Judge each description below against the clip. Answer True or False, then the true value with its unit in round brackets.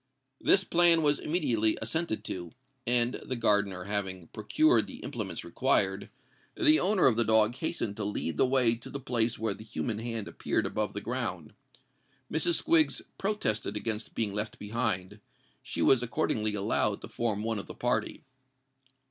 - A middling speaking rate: True (165 wpm)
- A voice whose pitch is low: True (115 Hz)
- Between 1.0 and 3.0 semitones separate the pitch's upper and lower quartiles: False (4.6 semitones)